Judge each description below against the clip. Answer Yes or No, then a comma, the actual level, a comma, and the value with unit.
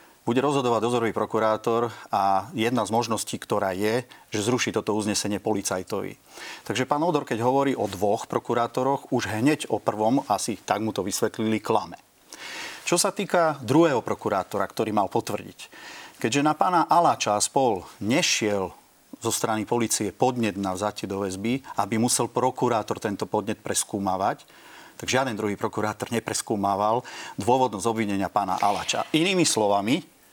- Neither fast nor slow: Yes, average, 140 wpm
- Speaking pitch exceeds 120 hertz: No, low, 115 Hz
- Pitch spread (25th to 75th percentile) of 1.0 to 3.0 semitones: No, average, 3.4 semitones